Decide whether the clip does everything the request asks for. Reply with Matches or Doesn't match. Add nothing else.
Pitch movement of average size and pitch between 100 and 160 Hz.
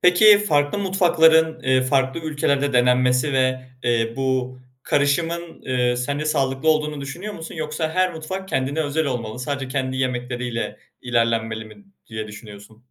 Matches